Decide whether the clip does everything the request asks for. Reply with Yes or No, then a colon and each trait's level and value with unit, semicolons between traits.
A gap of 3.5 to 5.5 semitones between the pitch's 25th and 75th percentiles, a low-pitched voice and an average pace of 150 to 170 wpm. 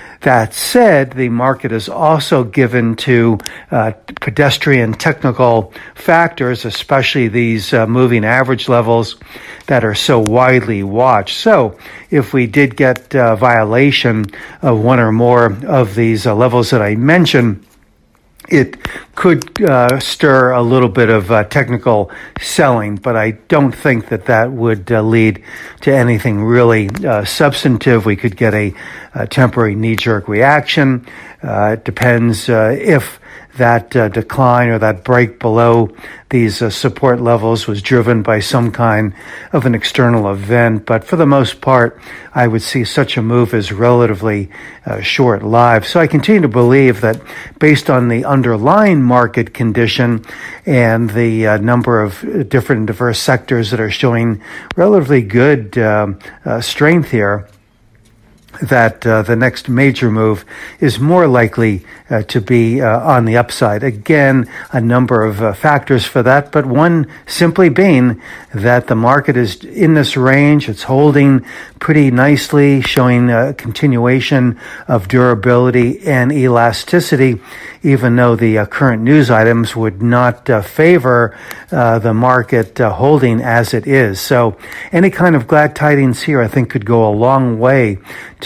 No: average, 3.0 semitones; low, 120 Hz; average, 155 wpm